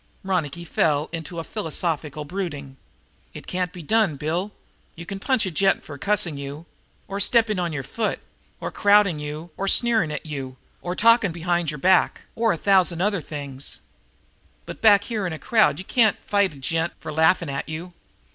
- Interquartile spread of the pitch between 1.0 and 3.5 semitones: No, average, 4.7 semitones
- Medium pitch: Yes, medium, 175 Hz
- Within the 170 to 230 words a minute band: Yes, average, 185 wpm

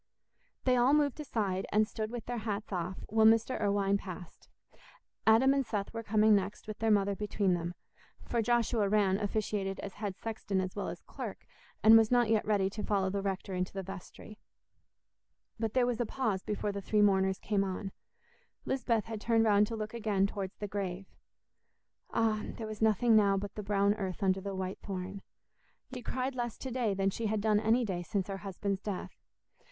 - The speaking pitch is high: Yes, high, 210 Hz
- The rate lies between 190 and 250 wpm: Yes, average, 200 wpm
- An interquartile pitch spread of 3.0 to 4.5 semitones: No, narrow, 2.4 semitones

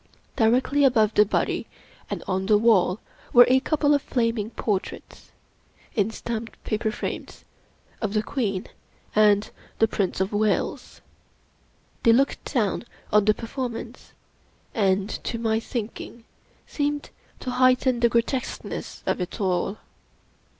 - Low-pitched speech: No, high, 225 Hz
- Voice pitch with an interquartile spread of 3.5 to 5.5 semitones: No, average, 3.0 semitones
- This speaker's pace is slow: Yes, slow, 130 wpm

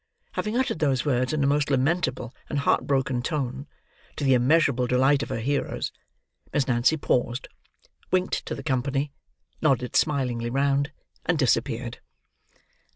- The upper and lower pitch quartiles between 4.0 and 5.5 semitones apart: No, average, 2.7 semitones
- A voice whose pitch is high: No, low, 135 Hz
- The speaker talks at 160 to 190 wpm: No, average, 145 wpm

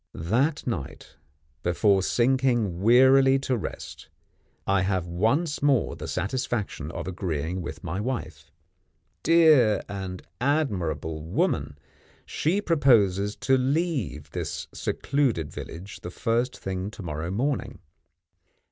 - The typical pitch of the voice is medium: No, low, 110 Hz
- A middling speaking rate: No, slow, 110 wpm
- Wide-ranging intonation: Yes, wide, 6.6 semitones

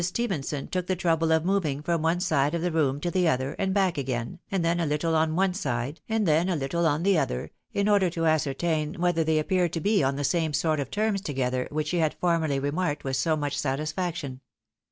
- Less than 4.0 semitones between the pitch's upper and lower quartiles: Yes, average, 3.6 semitones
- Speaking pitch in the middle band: Yes, medium, 160 Hz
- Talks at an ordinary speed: No, fast, 230 wpm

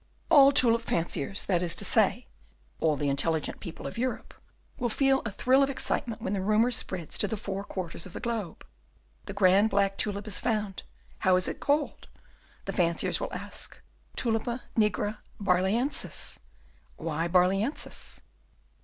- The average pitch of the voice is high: Yes, high, 200 Hz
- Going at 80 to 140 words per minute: No, average, 160 wpm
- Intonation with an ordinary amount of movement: Yes, average, 4.3 semitones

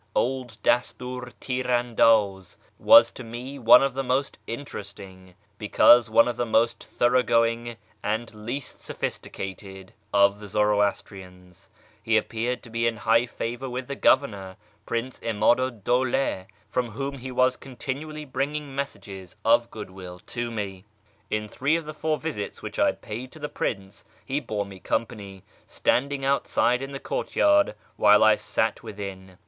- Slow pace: No, average, 155 wpm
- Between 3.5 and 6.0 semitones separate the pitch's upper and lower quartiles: Yes, average, 4.0 semitones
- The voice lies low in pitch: Yes, low, 115 Hz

